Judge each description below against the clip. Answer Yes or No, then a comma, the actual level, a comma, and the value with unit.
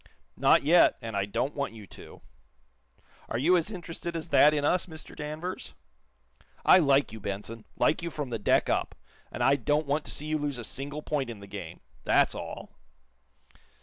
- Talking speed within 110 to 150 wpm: No, average, 190 wpm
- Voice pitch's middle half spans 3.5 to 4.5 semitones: No, wide, 5.5 semitones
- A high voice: No, medium, 145 Hz